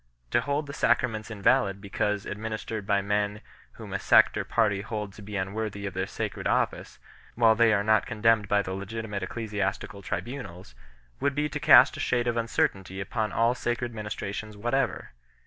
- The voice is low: Yes, low, 105 Hz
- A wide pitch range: No, average, 2.7 semitones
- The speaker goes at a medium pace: Yes, average, 175 wpm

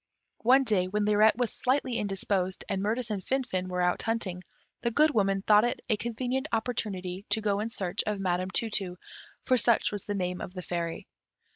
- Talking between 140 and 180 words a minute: No, average, 195 wpm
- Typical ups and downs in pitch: Yes, average, 3.8 semitones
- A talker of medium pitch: No, high, 210 Hz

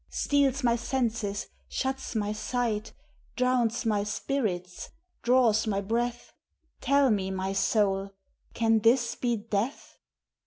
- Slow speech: Yes, slow, 115 wpm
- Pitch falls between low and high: No, high, 225 Hz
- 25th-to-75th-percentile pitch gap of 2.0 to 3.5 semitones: Yes, average, 3.2 semitones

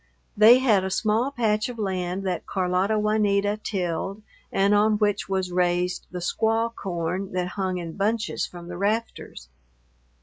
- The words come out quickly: No, average, 155 wpm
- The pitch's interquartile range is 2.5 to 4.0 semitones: Yes, average, 2.9 semitones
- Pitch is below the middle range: No, high, 195 Hz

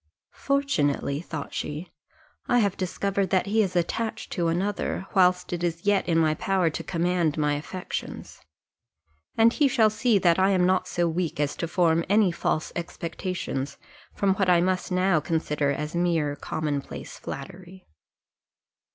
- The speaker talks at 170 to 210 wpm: No, average, 160 wpm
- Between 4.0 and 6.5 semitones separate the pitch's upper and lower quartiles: No, average, 3.1 semitones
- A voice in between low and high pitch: Yes, medium, 180 Hz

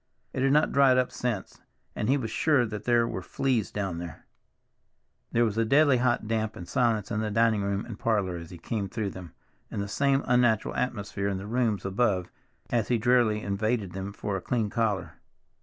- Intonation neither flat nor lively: Yes, average, 3.5 semitones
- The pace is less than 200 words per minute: No, fast, 205 wpm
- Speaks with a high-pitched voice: No, low, 110 Hz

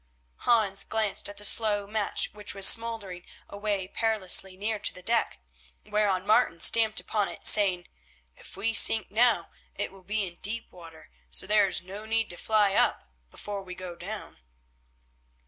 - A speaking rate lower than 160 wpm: No, average, 165 wpm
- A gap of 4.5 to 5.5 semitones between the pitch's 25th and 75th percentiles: No, narrow, 2.5 semitones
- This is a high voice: Yes, high, 205 Hz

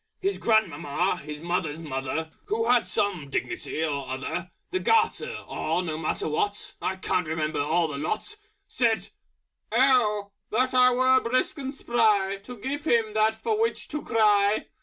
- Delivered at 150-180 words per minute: Yes, average, 160 wpm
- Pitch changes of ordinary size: No, wide, 7.6 semitones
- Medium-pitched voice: No, high, 210 Hz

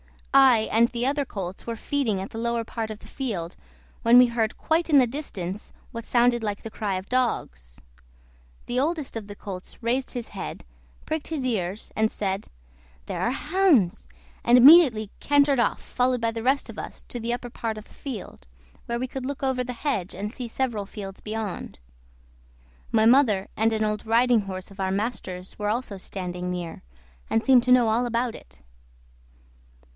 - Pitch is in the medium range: No, high, 230 Hz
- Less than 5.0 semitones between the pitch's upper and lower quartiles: Yes, average, 3.8 semitones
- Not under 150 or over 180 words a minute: No, average, 190 wpm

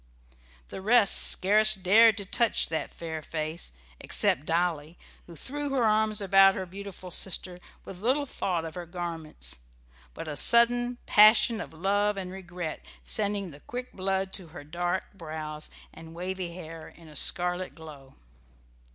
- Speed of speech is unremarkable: Yes, average, 150 wpm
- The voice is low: No, medium, 185 Hz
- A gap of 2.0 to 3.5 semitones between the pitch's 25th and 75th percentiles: No, average, 4.1 semitones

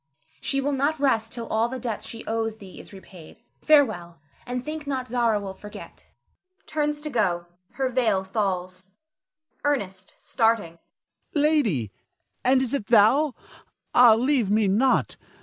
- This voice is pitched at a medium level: No, high, 230 Hz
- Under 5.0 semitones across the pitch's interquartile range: No, average, 5.3 semitones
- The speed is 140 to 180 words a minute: Yes, average, 145 wpm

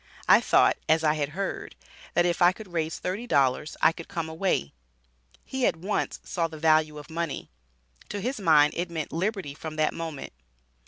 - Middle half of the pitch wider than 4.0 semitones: No, average, 2.9 semitones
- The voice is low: No, medium, 165 Hz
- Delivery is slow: No, average, 190 wpm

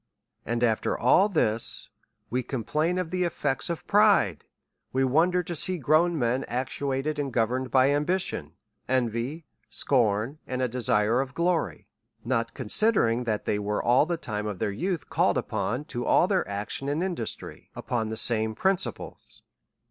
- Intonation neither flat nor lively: No, wide, 6.4 semitones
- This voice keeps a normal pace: Yes, average, 165 wpm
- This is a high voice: No, low, 130 Hz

